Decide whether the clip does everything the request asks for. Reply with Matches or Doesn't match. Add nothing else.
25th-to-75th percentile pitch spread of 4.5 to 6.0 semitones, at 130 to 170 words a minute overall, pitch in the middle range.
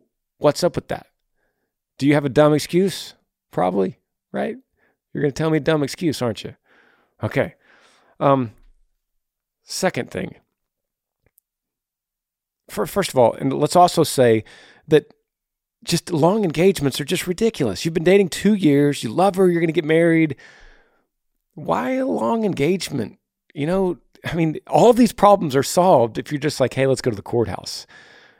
Matches